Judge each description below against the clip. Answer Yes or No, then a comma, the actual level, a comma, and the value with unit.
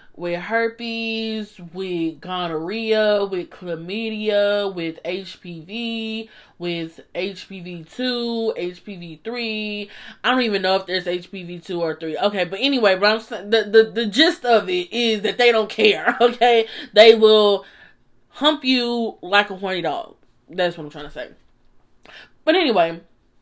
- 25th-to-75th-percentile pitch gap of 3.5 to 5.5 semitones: Yes, average, 4.3 semitones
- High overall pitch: Yes, high, 205 Hz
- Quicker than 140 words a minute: No, slow, 135 wpm